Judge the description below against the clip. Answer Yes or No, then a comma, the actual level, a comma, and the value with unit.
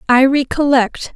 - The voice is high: Yes, very high, 275 Hz